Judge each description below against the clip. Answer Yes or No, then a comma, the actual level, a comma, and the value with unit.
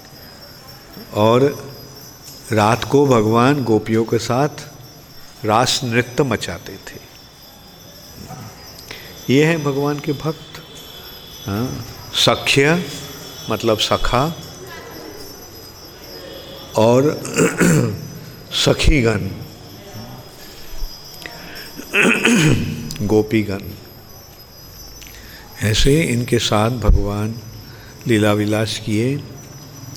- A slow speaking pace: Yes, slow, 60 wpm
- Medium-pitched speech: No, low, 120 Hz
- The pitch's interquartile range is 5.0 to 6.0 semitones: No, average, 4.3 semitones